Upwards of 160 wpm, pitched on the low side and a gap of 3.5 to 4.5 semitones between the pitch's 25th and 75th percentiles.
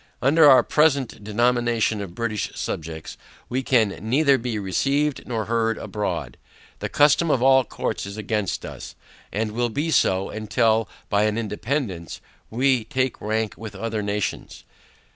No: average, 145 wpm; low, 115 Hz; average, 3.9 semitones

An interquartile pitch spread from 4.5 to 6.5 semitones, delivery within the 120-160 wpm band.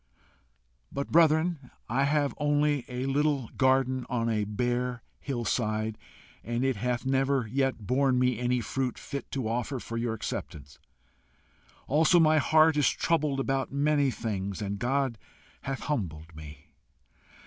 No: average, 3.4 semitones; average, 140 wpm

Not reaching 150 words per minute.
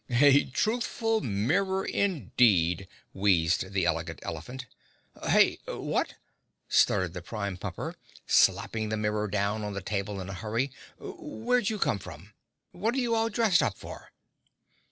Yes: average, 140 wpm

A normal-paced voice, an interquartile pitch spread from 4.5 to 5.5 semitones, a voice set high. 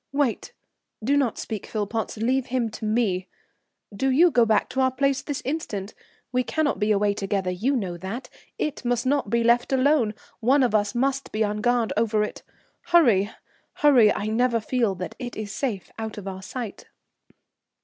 No: average, 180 wpm; average, 3.9 semitones; high, 230 Hz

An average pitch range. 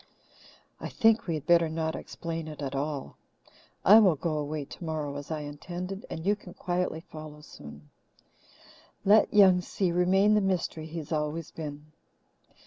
Yes: average, 3.3 semitones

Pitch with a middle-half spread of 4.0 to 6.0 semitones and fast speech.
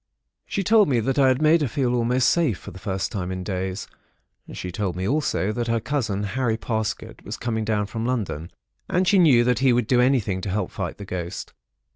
Yes: average, 4.8 semitones; fast, 220 wpm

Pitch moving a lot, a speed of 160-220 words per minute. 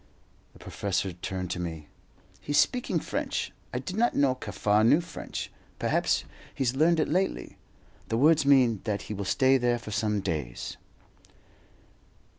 No: wide, 6.6 semitones; average, 150 wpm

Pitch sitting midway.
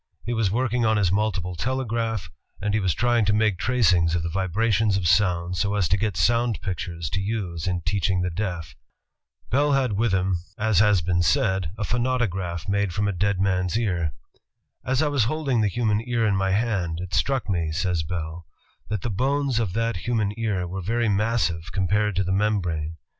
No: low, 100 Hz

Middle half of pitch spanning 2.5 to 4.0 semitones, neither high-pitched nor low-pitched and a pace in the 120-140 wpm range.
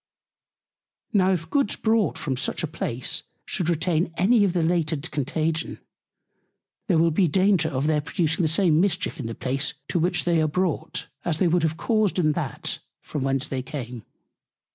No: average, 3.3 semitones; medium, 165 Hz; average, 180 wpm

